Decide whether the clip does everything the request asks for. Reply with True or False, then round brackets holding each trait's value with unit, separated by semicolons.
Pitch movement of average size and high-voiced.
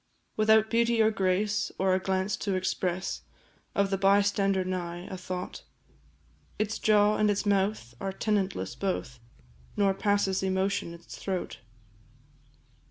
False (1.8 semitones; 195 Hz)